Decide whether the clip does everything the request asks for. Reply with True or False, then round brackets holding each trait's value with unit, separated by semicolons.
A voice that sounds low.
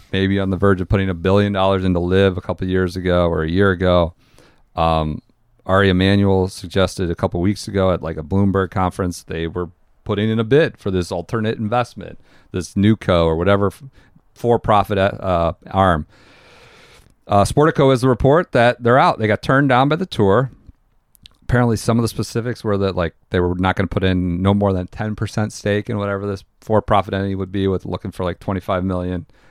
True (95 Hz)